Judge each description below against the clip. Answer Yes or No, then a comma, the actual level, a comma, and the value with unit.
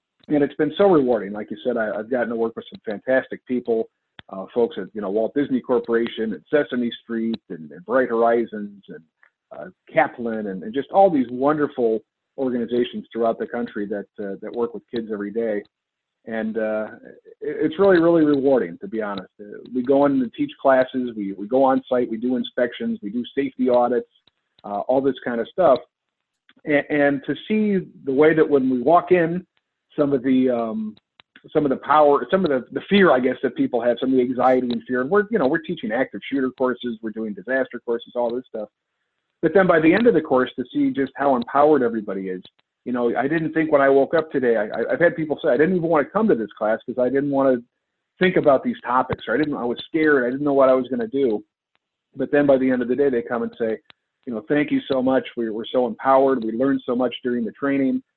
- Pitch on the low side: Yes, low, 130 Hz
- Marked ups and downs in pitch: No, average, 3.7 semitones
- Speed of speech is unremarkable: No, fast, 235 wpm